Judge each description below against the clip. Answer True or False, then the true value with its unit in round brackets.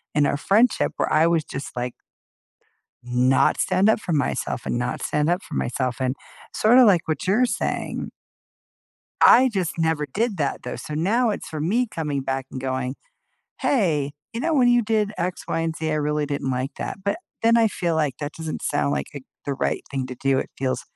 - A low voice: False (155 Hz)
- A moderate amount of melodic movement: False (7.0 semitones)